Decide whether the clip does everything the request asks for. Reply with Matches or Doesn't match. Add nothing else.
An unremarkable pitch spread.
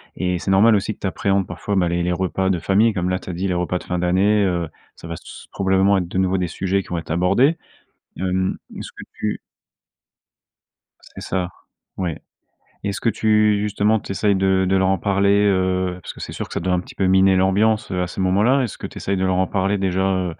Doesn't match